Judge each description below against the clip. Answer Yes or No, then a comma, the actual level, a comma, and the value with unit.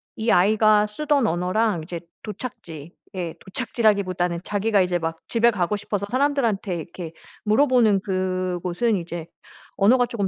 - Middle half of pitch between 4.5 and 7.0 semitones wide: No, average, 4.1 semitones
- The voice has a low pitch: No, high, 200 Hz